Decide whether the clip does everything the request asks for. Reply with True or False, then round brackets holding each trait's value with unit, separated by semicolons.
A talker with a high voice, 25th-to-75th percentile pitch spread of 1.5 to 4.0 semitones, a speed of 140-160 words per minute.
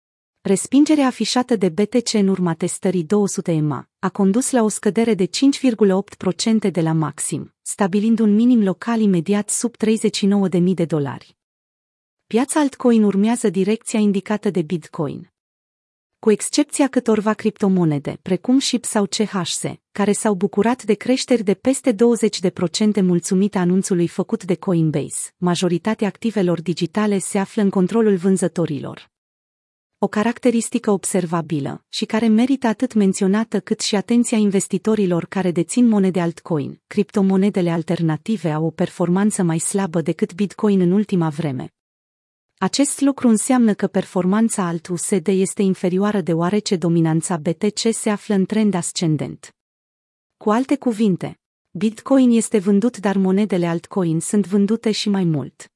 False (200 Hz; 3.7 semitones; 130 wpm)